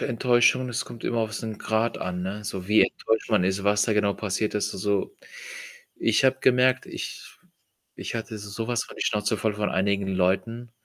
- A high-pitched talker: No, low, 105 Hz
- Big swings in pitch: No, average, 2.7 semitones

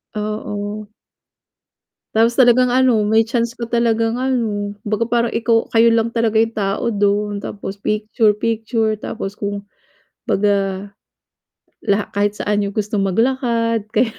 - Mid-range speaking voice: No, high, 220 Hz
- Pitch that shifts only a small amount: Yes, narrow, 2.1 semitones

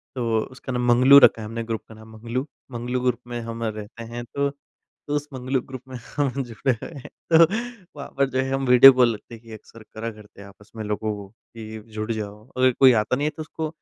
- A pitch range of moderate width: Yes, average, 3.3 semitones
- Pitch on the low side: Yes, low, 120 Hz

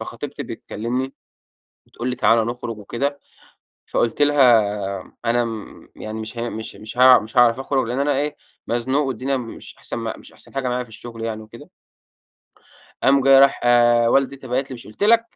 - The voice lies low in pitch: Yes, low, 125 Hz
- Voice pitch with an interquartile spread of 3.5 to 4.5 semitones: No, average, 2.9 semitones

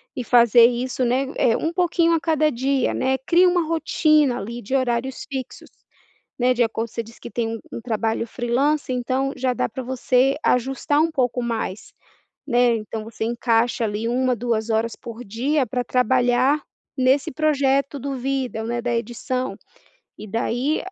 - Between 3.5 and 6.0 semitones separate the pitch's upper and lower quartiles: No, average, 2.7 semitones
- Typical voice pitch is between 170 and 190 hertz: No, very high, 250 Hz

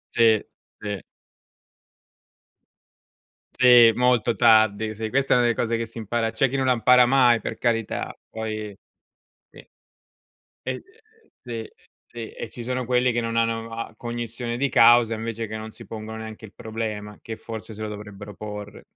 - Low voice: Yes, low, 115 Hz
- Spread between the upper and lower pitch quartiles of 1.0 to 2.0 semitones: Yes, narrow, 1.6 semitones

